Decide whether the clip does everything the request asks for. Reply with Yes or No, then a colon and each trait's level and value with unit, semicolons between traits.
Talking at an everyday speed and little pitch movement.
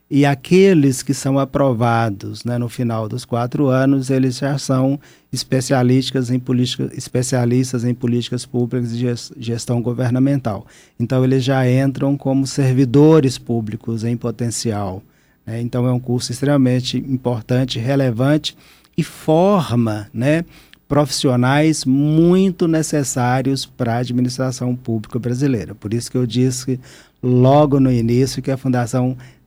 Yes: average, 130 wpm; narrow, 2.2 semitones